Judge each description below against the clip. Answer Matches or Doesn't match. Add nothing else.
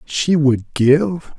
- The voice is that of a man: Matches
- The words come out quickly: Doesn't match